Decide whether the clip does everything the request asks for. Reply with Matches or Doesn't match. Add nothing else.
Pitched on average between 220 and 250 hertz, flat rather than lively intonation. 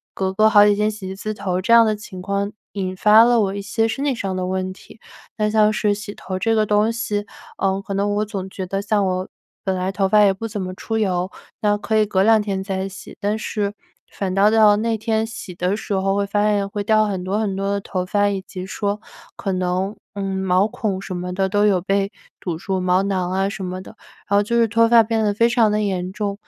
Doesn't match